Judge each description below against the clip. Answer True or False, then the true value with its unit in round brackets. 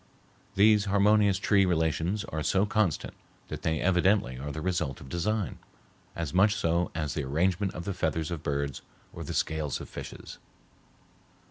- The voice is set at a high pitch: False (85 Hz)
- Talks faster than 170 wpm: False (160 wpm)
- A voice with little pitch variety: False (4.2 semitones)